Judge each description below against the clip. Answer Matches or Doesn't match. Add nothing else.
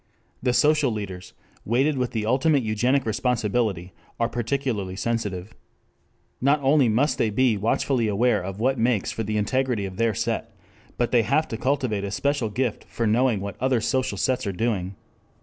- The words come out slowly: Doesn't match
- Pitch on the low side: Matches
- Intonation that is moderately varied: Matches